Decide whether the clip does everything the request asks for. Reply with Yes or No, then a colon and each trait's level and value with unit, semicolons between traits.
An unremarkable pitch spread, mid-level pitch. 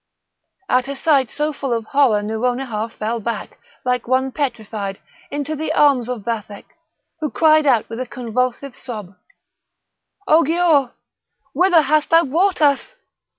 No: average, 4.5 semitones; very high, 260 Hz